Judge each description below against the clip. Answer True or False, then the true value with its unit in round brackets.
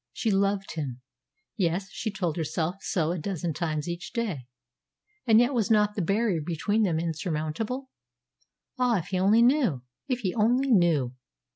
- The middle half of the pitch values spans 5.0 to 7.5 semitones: True (5.4 semitones)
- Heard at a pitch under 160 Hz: False (190 Hz)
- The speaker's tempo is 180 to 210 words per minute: False (160 wpm)